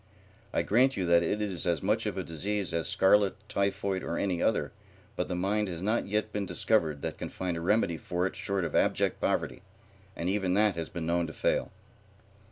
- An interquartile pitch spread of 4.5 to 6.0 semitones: No, average, 3.4 semitones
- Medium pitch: No, very low, 95 Hz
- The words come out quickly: Yes, fast, 210 wpm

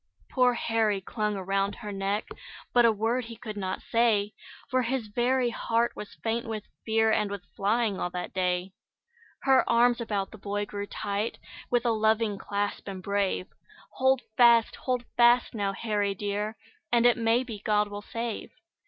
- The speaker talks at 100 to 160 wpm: No, average, 170 wpm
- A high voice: Yes, high, 220 Hz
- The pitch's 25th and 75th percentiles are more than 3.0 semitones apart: No, average, 2.7 semitones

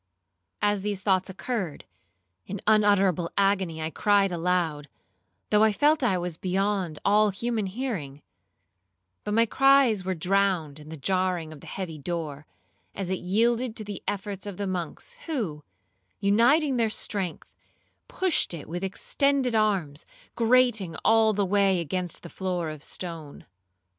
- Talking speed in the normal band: Yes, average, 145 wpm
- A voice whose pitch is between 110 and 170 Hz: No, high, 195 Hz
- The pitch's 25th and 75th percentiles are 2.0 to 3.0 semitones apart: No, average, 3.8 semitones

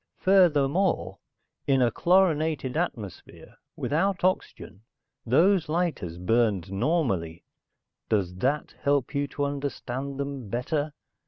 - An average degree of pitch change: No, wide, 5.7 semitones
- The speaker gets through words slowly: Yes, slow, 100 wpm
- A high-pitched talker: No, medium, 140 Hz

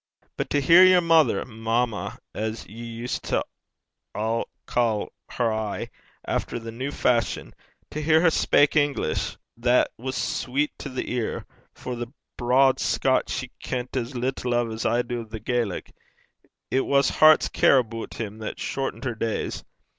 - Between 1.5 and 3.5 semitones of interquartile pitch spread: Yes, average, 2.8 semitones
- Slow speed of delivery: No, average, 160 wpm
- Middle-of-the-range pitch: No, low, 120 Hz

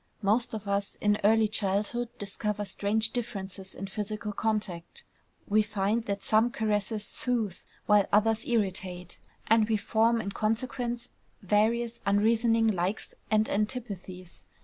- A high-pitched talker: Yes, high, 215 Hz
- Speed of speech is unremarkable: No, slow, 125 wpm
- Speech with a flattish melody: Yes, narrow, 2.1 semitones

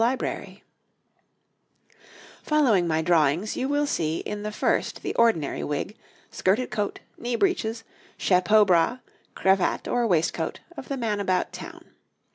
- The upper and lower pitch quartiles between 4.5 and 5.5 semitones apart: Yes, average, 5.2 semitones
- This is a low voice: No, high, 210 Hz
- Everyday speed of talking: No, slow, 130 wpm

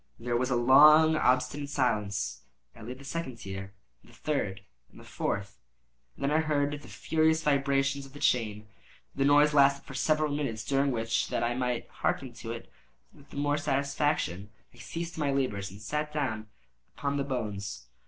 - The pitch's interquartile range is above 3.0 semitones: Yes, average, 4.3 semitones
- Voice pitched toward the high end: No, low, 135 Hz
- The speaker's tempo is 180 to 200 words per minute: Yes, average, 190 wpm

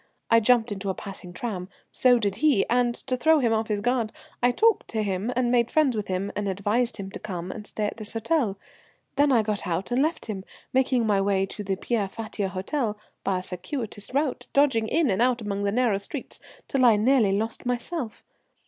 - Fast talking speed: Yes, fast, 215 wpm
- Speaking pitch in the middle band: No, high, 220 Hz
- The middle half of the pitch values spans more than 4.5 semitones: No, average, 3.8 semitones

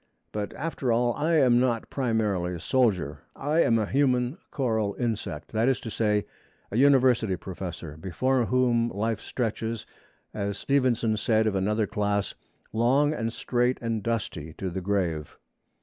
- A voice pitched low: Yes, low, 115 Hz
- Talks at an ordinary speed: Yes, average, 150 wpm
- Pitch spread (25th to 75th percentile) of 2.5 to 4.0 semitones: Yes, average, 3.7 semitones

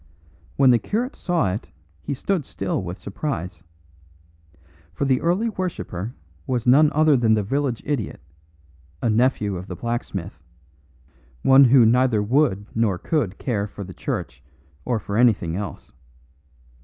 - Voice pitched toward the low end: Yes, low, 120 Hz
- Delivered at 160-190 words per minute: No, average, 145 wpm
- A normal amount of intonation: No, wide, 5.9 semitones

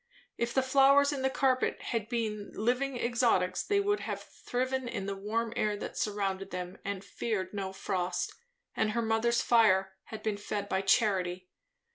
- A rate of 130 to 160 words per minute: No, average, 170 wpm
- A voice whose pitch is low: No, high, 220 Hz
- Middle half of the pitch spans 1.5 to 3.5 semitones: No, average, 4.0 semitones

